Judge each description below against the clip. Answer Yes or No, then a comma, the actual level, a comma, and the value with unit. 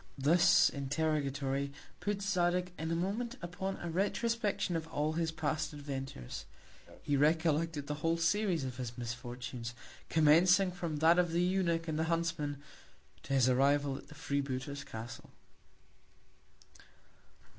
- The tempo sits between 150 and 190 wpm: No, slow, 135 wpm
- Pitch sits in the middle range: Yes, medium, 160 Hz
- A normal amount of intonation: Yes, average, 3.8 semitones